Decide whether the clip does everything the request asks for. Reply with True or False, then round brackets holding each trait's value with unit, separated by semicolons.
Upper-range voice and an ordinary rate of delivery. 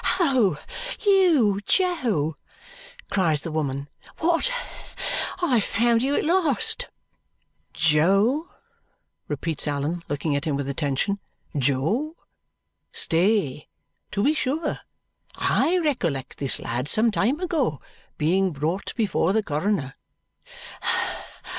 False (195 Hz; 105 wpm)